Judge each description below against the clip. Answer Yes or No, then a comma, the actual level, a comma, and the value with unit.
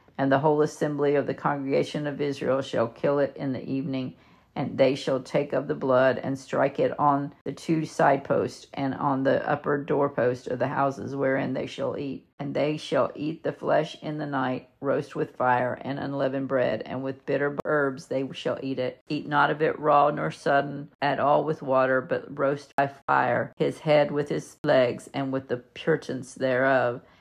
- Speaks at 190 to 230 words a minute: Yes, average, 200 wpm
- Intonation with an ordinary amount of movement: No, narrow, 1.7 semitones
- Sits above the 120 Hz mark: Yes, low, 135 Hz